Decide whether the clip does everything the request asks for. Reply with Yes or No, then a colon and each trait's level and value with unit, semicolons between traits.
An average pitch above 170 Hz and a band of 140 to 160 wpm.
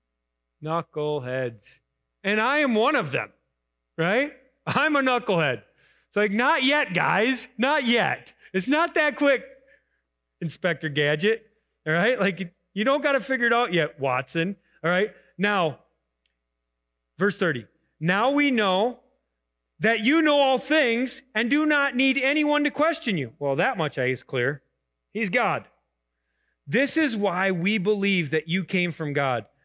Yes: high, 190 Hz; average, 150 wpm